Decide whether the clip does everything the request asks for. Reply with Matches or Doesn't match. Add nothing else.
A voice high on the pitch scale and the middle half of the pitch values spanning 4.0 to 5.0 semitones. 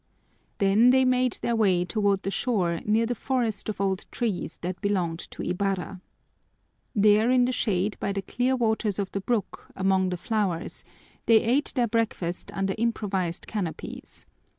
Doesn't match